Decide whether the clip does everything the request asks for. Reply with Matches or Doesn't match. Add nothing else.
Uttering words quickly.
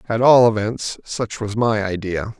Doesn't match